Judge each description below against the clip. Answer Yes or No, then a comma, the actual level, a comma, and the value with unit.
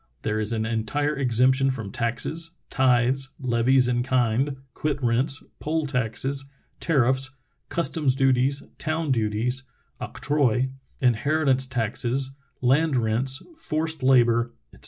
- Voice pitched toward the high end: No, low, 130 Hz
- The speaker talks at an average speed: No, slow, 115 wpm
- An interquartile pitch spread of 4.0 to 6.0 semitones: No, average, 2.7 semitones